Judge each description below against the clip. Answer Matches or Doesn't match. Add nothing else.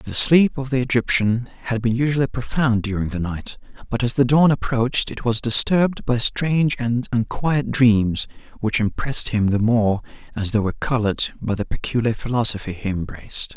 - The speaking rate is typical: Matches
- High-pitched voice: Doesn't match